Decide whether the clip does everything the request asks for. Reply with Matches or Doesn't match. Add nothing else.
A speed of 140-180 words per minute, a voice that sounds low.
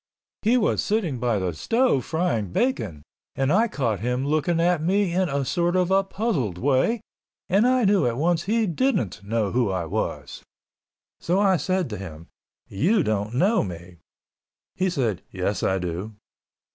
Doesn't match